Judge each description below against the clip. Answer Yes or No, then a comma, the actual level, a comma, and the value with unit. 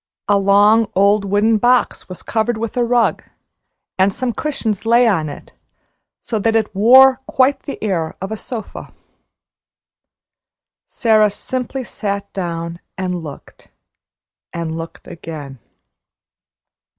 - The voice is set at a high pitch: Yes, high, 210 Hz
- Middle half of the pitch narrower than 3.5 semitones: No, average, 4.3 semitones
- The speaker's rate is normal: No, slow, 125 wpm